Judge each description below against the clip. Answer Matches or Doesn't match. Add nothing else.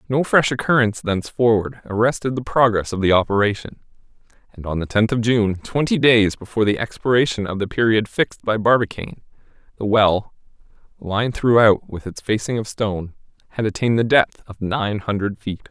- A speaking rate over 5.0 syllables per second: Matches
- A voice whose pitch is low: Matches